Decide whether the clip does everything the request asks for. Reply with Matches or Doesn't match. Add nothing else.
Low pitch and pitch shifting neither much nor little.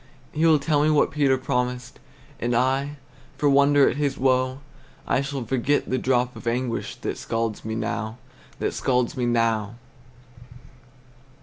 Matches